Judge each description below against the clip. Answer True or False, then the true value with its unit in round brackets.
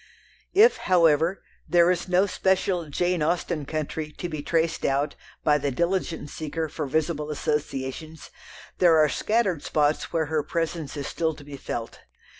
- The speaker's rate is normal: True (155 wpm)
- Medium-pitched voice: True (160 Hz)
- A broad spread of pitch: False (2.8 semitones)